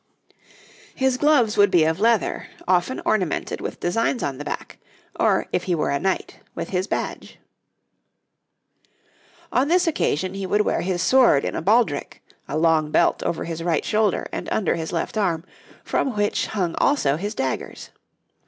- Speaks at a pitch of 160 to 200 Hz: Yes, medium, 185 Hz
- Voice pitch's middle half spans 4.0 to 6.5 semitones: Yes, average, 5.2 semitones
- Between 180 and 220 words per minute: No, average, 165 wpm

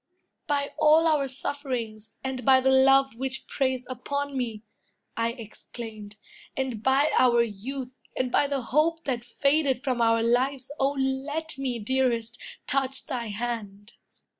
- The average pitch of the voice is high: Yes, very high, 260 Hz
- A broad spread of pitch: No, average, 2.7 semitones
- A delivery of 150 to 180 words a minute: No, average, 140 wpm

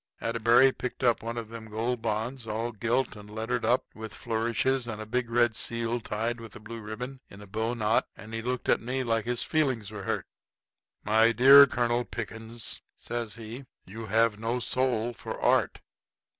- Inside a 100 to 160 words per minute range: No, average, 185 wpm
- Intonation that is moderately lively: No, narrow, 1.7 semitones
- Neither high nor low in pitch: No, low, 115 Hz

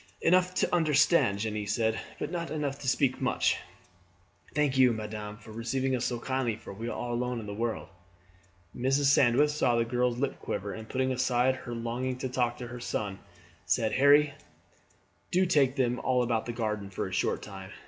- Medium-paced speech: Yes, average, 195 wpm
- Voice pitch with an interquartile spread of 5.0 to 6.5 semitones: No, average, 3.3 semitones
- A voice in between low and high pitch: No, low, 125 Hz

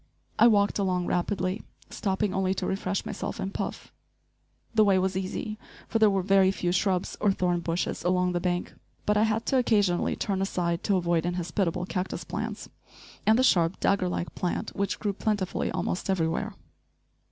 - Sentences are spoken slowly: No, average, 175 wpm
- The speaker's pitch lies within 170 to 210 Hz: Yes, high, 190 Hz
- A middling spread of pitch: No, narrow, 2.3 semitones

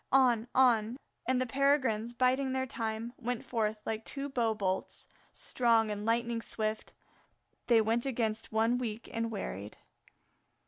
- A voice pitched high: Yes, high, 230 Hz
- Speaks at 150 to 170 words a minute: No, average, 140 wpm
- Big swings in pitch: No, narrow, 2.5 semitones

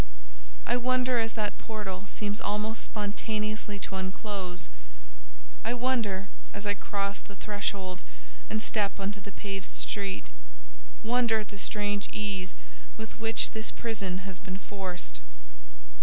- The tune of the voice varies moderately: No, narrow, 2.3 semitones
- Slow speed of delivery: Yes, slow, 125 wpm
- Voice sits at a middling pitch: No, high, 205 Hz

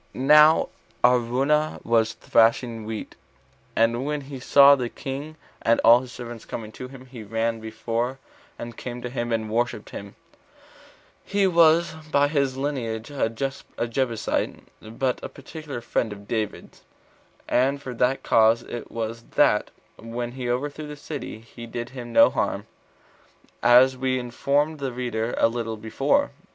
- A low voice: Yes, low, 125 Hz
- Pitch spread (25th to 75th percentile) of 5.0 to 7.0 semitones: No, average, 3.2 semitones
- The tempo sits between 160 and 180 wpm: No, average, 150 wpm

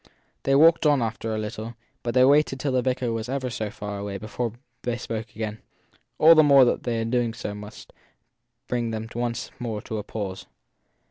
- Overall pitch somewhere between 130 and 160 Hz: No, low, 115 Hz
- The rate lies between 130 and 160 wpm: No, average, 195 wpm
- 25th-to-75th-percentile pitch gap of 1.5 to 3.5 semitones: Yes, average, 2.8 semitones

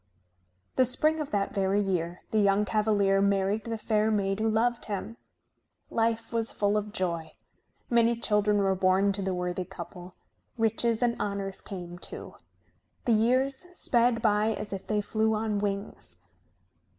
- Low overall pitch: No, high, 210 Hz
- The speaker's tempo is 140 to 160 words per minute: Yes, average, 155 wpm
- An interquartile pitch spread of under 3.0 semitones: Yes, narrow, 2.5 semitones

